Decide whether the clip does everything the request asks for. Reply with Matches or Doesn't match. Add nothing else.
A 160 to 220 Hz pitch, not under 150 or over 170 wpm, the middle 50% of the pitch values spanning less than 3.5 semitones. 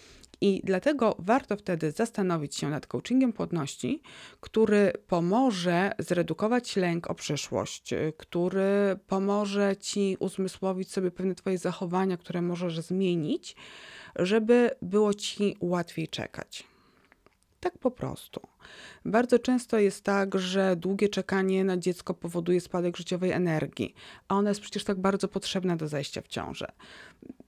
Doesn't match